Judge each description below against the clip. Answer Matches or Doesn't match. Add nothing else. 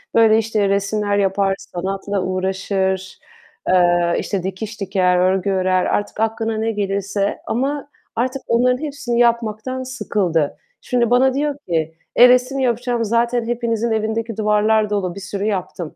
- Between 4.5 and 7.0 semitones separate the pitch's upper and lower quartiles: Doesn't match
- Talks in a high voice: Matches